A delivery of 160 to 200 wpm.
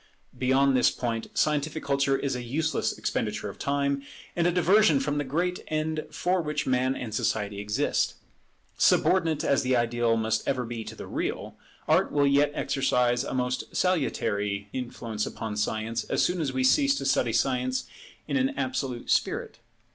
Yes: average, 170 wpm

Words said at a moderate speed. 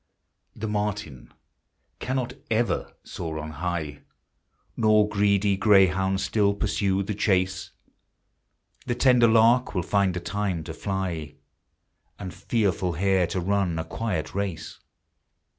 No: slow, 120 wpm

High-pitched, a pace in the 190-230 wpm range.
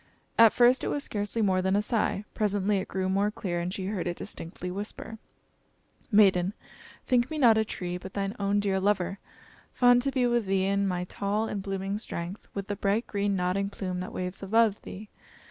Yes: high, 200 Hz; average, 200 wpm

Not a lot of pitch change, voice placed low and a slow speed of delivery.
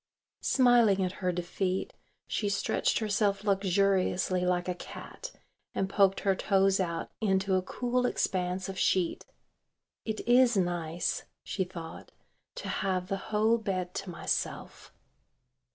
No: narrow, 2.3 semitones; high, 195 Hz; slow, 130 wpm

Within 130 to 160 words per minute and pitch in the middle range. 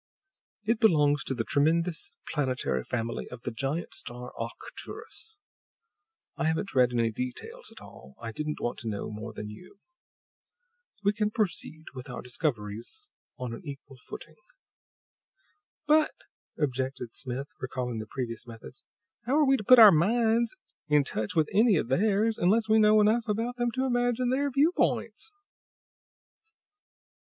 Yes: average, 145 wpm; medium, 155 Hz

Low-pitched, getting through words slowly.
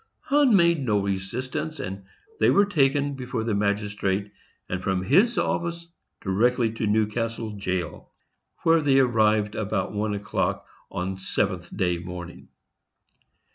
Yes: low, 110 Hz; slow, 130 wpm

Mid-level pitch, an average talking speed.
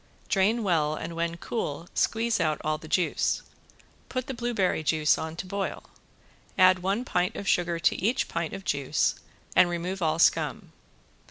Yes: medium, 180 Hz; average, 165 wpm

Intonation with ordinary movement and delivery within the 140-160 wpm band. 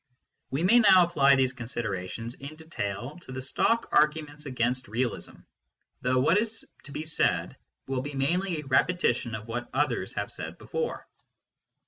Yes: average, 4.7 semitones; average, 155 wpm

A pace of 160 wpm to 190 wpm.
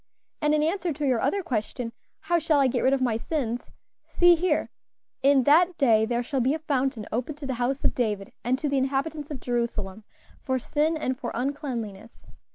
No: average, 200 wpm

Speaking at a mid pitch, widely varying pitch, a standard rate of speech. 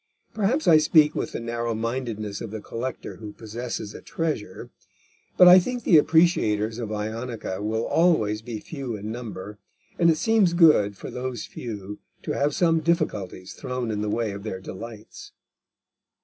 No: low, 115 Hz; wide, 6.8 semitones; average, 165 wpm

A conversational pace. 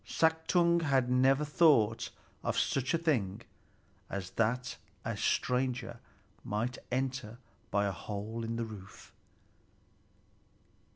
No: slow, 110 wpm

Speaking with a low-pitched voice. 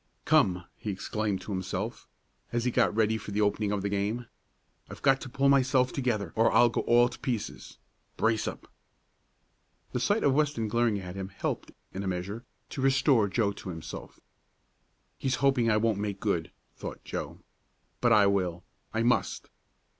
Yes: low, 110 Hz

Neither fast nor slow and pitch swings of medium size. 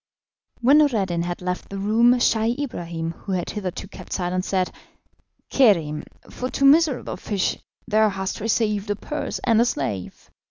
Yes: average, 155 wpm; average, 4.7 semitones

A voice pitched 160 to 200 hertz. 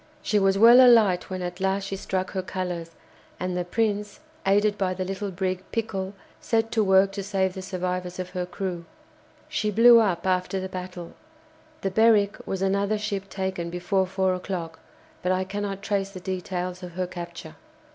Yes: high, 190 Hz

